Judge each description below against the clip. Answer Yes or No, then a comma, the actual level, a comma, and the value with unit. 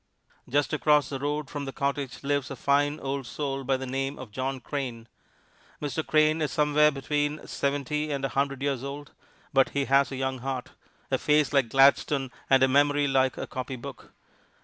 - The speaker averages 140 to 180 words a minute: No, average, 190 wpm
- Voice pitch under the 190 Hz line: Yes, medium, 140 Hz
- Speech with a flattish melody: Yes, narrow, 1.6 semitones